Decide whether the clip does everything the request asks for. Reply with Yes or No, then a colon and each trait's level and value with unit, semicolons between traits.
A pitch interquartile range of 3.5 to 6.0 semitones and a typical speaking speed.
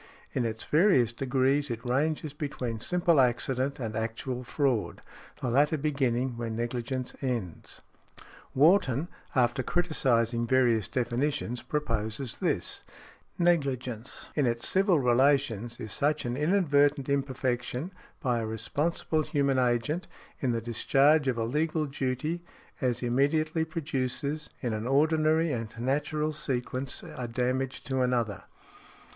No: average, 3.8 semitones; slow, 125 wpm